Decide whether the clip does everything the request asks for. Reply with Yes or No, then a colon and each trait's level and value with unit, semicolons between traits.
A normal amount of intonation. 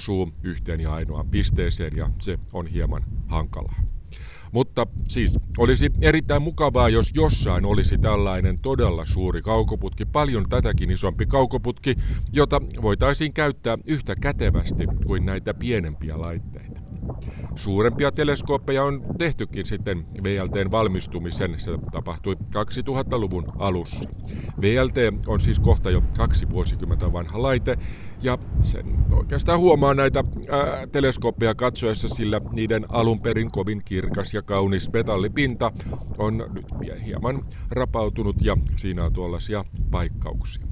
Yes: average, 4.5 semitones